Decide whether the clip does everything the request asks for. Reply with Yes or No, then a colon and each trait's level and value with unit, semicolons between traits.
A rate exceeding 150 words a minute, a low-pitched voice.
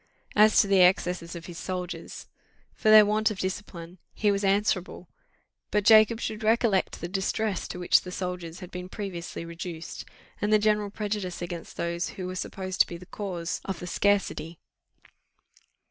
No: average, 170 wpm; medium, 185 Hz